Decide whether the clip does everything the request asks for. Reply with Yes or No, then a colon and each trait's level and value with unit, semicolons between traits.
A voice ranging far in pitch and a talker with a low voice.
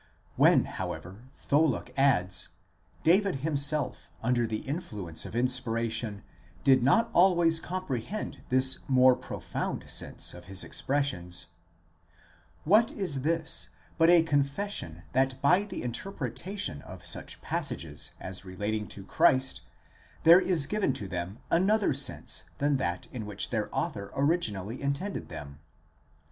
Yes: wide, 7.8 semitones; low, 130 Hz